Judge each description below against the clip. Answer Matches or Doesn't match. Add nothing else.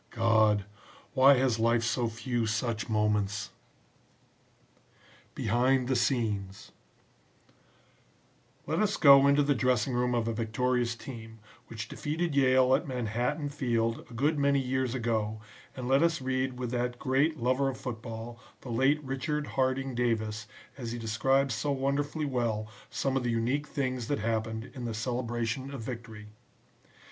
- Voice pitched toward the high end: Doesn't match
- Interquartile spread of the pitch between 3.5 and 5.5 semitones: Doesn't match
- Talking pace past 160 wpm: Doesn't match